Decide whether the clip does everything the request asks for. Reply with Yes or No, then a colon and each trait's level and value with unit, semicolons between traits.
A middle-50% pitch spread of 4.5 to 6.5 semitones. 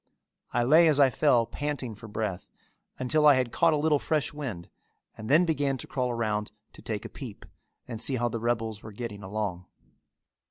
Yes: average, 5.0 semitones